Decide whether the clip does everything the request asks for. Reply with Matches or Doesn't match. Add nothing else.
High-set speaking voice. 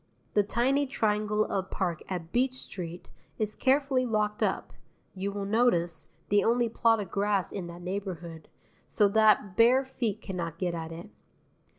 Matches